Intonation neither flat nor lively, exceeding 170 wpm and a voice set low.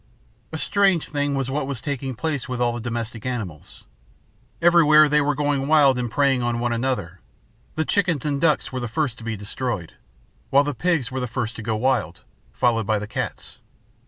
Yes: average, 3.9 semitones; average, 195 wpm; low, 130 Hz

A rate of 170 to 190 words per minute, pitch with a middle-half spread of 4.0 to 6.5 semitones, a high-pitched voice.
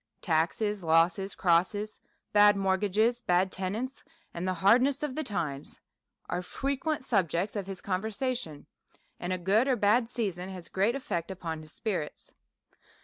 No: average, 155 wpm; average, 4.4 semitones; high, 195 Hz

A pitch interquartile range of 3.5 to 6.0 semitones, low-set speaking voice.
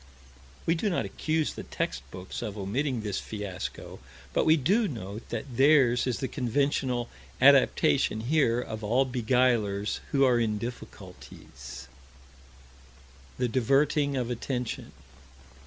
Yes: average, 4.5 semitones; low, 125 Hz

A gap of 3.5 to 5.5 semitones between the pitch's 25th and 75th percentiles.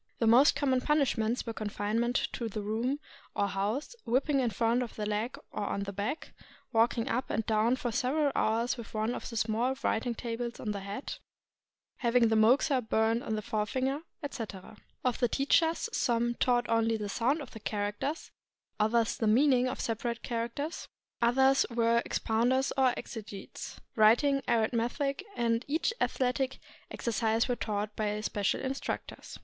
No: average, 2.9 semitones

